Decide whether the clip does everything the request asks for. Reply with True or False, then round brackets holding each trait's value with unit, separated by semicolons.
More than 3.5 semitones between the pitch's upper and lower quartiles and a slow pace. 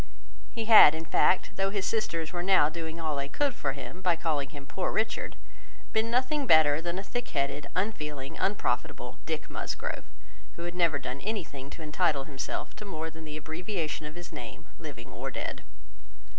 False (4.9 semitones; 185 wpm)